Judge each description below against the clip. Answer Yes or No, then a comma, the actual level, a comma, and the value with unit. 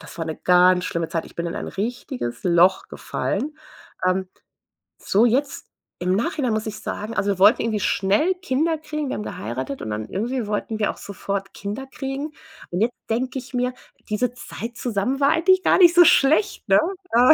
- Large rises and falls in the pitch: Yes, wide, 6.1 semitones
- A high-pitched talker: Yes, high, 220 Hz